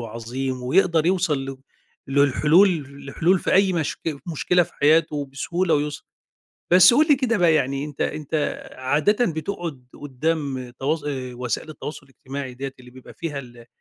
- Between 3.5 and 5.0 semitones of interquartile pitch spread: Yes, average, 4.2 semitones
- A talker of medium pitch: Yes, medium, 150 Hz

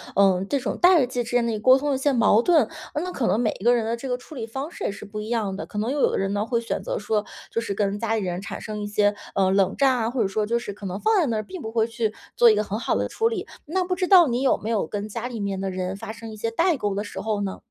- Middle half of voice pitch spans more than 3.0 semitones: Yes, average, 4.1 semitones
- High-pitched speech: Yes, high, 225 Hz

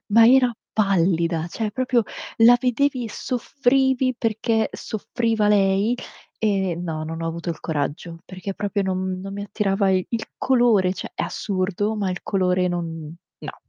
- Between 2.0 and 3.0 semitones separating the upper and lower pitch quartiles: No, average, 4.0 semitones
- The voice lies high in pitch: Yes, high, 200 Hz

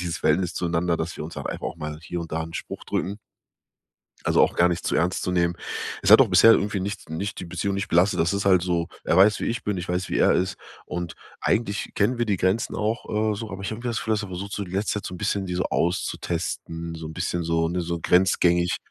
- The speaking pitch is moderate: No, very low, 90 Hz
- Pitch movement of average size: Yes, average, 3.0 semitones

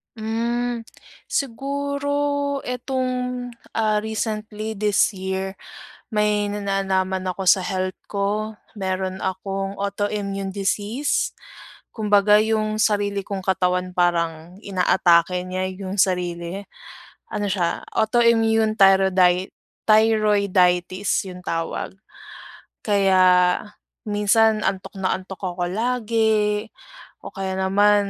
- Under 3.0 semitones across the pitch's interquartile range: Yes, narrow, 2.6 semitones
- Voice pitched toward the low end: No, high, 200 Hz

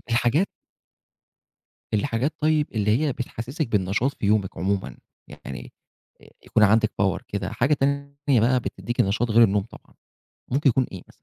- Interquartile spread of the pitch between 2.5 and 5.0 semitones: No, wide, 5.5 semitones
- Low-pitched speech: Yes, low, 115 Hz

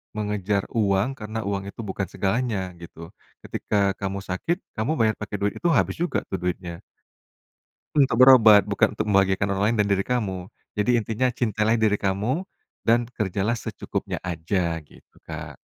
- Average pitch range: Yes, average, 3.0 semitones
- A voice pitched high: No, low, 105 Hz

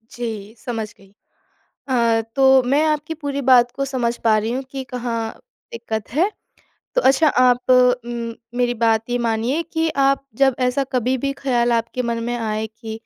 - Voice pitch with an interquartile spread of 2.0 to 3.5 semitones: Yes, average, 2.8 semitones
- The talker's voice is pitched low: No, high, 245 Hz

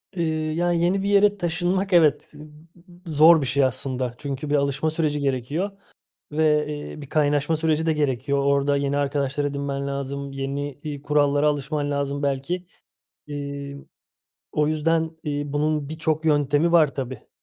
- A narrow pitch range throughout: Yes, narrow, 2.1 semitones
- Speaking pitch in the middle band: Yes, medium, 145 Hz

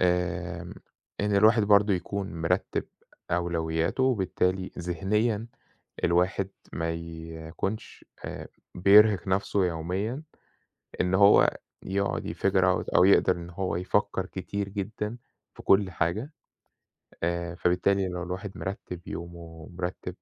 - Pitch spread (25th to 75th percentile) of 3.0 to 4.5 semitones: No, narrow, 2.6 semitones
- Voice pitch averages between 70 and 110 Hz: Yes, very low, 95 Hz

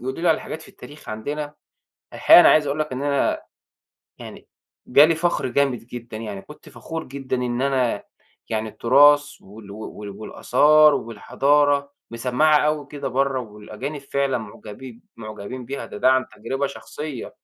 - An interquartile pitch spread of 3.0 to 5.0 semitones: Yes, average, 4.2 semitones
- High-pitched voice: No, low, 130 Hz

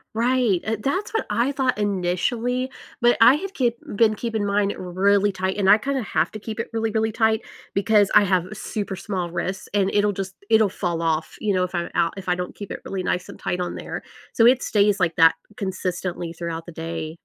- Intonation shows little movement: No, average, 3.8 semitones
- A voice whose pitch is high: Yes, high, 200 Hz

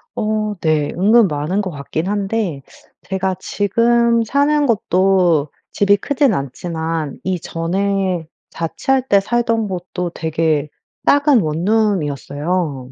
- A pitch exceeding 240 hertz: No, high, 190 Hz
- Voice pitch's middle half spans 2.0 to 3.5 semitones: No, average, 5.1 semitones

